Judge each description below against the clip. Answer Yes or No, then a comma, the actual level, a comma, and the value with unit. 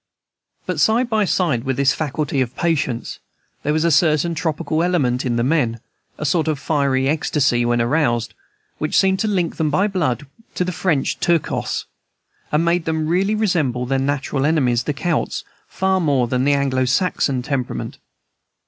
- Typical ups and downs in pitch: Yes, average, 4.6 semitones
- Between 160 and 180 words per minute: Yes, average, 170 wpm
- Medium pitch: Yes, medium, 150 Hz